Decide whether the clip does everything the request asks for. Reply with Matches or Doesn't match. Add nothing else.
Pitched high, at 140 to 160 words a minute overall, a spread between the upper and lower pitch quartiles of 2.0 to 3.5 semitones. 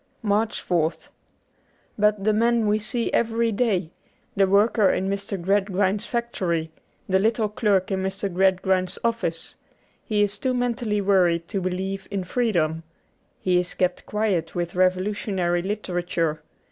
Matches